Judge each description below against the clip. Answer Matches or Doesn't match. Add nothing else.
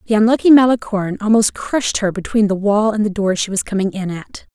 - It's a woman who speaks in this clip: Matches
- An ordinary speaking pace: Doesn't match